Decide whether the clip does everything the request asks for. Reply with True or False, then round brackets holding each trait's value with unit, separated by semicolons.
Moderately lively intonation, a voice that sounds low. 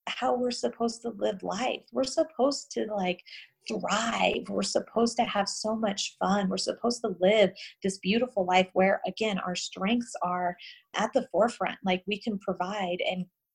False (4.1 semitones; 205 Hz)